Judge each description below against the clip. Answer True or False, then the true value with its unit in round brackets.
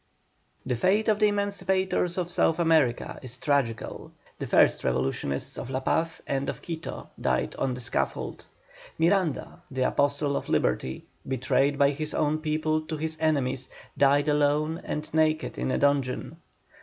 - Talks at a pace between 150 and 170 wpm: True (155 wpm)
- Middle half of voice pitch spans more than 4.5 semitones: False (3.5 semitones)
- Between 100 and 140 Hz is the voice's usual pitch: False (150 Hz)